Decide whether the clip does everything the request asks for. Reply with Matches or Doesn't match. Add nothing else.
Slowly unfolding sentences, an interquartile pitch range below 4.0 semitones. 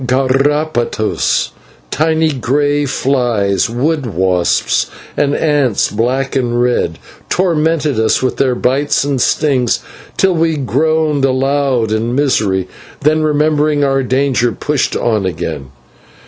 Matches